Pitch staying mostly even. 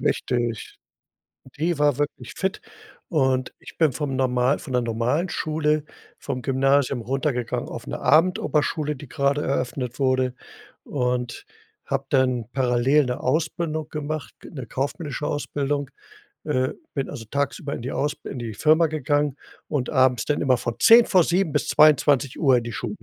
No: average, 3.1 semitones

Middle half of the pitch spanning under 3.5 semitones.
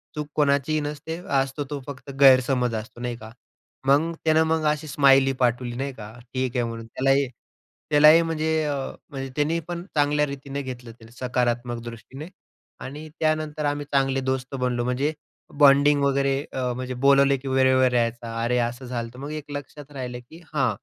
Yes: average, 2.9 semitones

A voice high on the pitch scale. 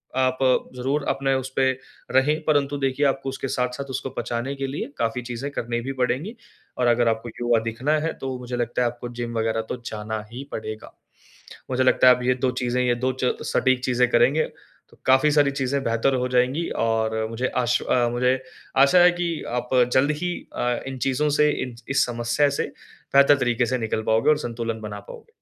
No: low, 125 Hz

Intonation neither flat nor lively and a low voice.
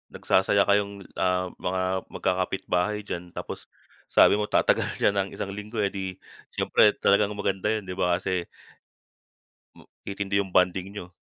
No: narrow, 1.7 semitones; very low, 95 Hz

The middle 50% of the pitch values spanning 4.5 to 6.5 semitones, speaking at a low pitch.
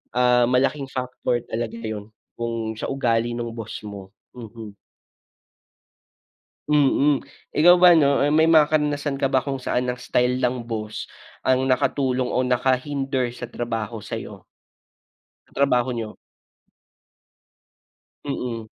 No: average, 3.0 semitones; low, 125 Hz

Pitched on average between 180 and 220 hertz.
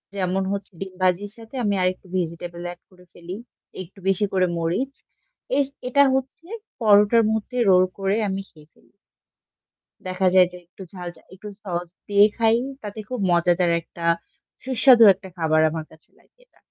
Yes: high, 190 Hz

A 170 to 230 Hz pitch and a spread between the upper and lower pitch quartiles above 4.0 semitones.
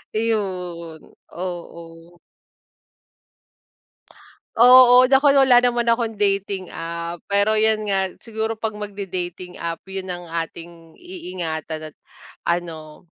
Yes: high, 190 Hz; average, 4.6 semitones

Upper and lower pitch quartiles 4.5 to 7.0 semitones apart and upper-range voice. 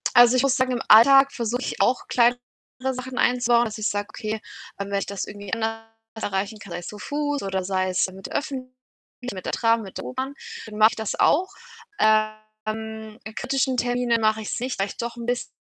No: average, 2.8 semitones; high, 225 Hz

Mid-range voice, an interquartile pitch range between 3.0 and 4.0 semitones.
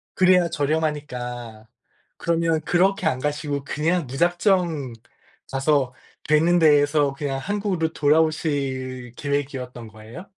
Yes: medium, 150 Hz; average, 3.7 semitones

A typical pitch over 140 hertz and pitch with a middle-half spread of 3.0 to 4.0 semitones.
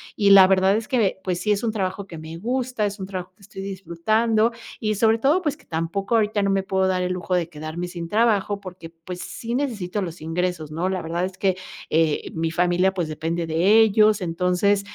Yes: high, 190 Hz; average, 3.5 semitones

